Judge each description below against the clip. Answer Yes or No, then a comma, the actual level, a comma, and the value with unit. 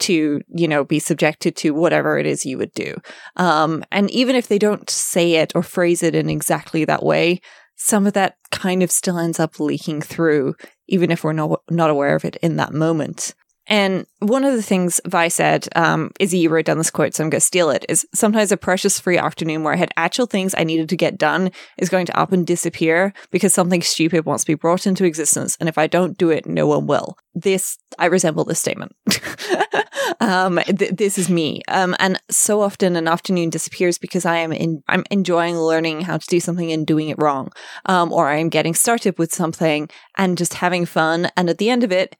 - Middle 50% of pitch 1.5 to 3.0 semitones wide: Yes, average, 2.7 semitones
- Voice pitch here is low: No, medium, 175 Hz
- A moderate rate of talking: No, fast, 225 wpm